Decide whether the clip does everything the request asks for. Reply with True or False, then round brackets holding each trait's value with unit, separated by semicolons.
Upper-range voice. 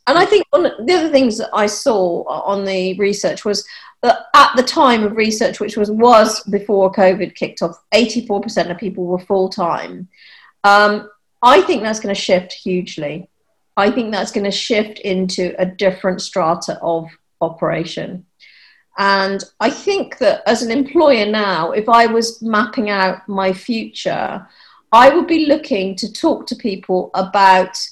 True (205 Hz)